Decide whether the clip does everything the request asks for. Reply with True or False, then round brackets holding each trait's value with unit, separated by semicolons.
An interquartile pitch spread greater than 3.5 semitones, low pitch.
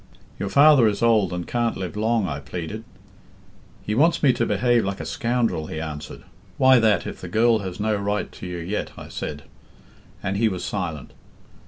True (4.4 semitones; 105 Hz)